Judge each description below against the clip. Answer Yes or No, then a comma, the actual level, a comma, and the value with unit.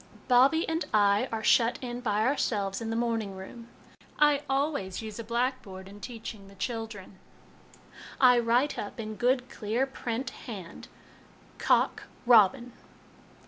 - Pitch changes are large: No, average, 3.4 semitones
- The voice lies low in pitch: No, high, 230 Hz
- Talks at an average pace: Yes, average, 150 wpm